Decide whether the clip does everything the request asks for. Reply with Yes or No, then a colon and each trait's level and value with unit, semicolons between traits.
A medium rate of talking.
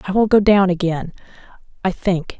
Yes: average, 175 wpm